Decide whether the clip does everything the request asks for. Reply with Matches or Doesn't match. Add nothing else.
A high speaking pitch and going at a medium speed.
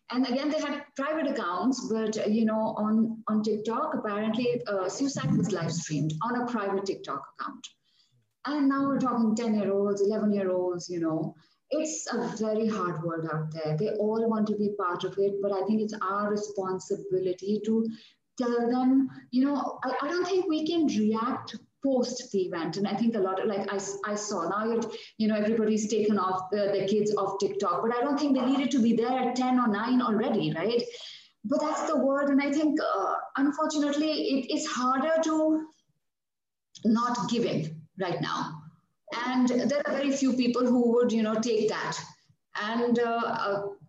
Matches